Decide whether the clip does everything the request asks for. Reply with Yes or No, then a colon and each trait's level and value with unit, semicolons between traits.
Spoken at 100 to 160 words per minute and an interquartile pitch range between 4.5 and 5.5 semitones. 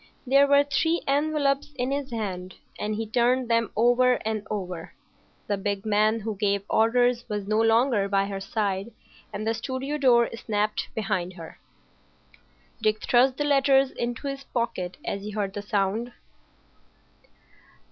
No: average, 150 wpm; average, 4.1 semitones